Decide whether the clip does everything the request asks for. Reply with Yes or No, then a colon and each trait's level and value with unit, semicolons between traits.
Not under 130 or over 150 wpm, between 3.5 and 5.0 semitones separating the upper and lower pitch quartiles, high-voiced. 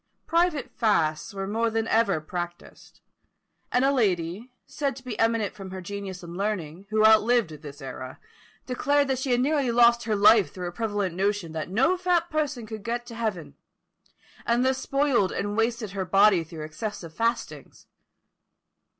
No: average, 165 wpm; average, 4.7 semitones; high, 215 Hz